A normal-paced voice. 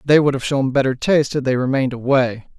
No: fast, 230 wpm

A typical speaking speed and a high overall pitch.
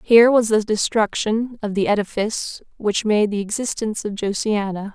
Yes: average, 160 wpm; high, 215 Hz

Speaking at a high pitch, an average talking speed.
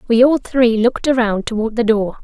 No: high, 235 Hz; fast, 215 wpm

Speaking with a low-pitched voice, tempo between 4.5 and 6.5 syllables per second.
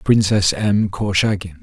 No: very low, 95 Hz; 4.0 syllables/s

